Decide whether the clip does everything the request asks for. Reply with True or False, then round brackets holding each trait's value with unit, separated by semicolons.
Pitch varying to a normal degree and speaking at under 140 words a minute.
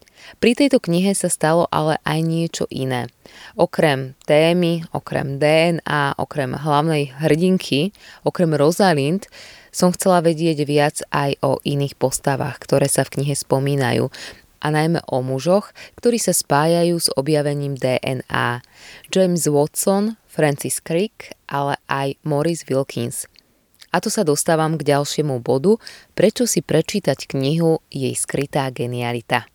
True (3.7 semitones; 130 wpm)